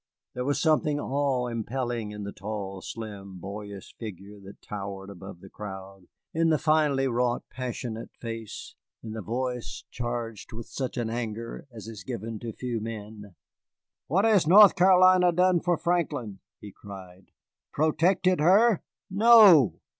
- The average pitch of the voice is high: No, low, 120 Hz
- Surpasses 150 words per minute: No, average, 145 wpm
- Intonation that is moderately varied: No, wide, 7.0 semitones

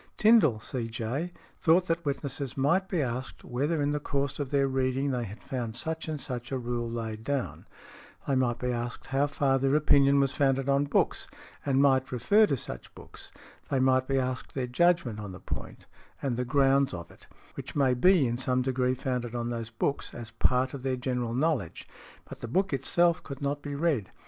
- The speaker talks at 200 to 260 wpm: Yes, fast, 205 wpm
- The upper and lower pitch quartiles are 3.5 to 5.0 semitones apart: No, average, 2.7 semitones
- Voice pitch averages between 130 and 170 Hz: Yes, low, 135 Hz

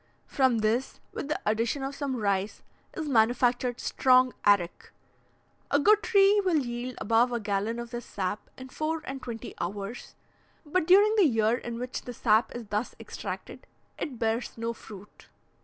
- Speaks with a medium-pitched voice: No, high, 240 Hz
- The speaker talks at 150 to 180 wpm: Yes, average, 165 wpm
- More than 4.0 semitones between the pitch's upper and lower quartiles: No, average, 3.7 semitones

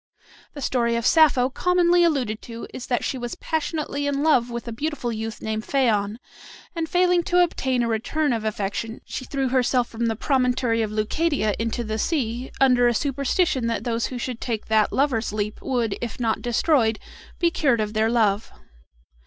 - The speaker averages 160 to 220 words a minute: Yes, average, 185 wpm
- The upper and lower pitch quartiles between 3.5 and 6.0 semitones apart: Yes, average, 4.0 semitones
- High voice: Yes, high, 245 Hz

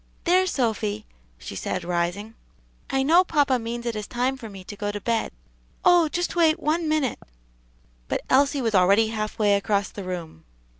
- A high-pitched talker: Yes, high, 225 Hz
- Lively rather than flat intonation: Yes, wide, 6.0 semitones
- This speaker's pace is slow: No, average, 180 wpm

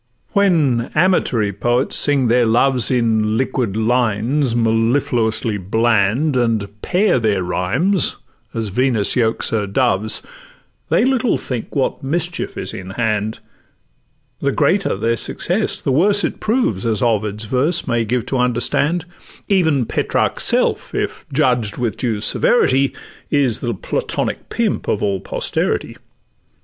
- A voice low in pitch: Yes, low, 120 Hz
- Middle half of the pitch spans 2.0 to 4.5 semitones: Yes, average, 4.0 semitones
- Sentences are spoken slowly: Yes, slow, 130 wpm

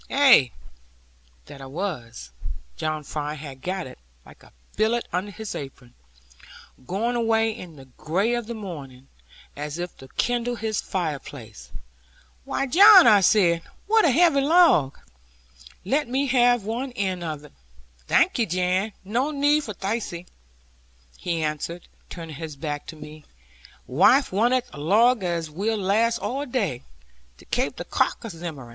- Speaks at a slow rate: No, average, 150 wpm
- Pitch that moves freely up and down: Yes, wide, 7.6 semitones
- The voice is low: No, high, 195 Hz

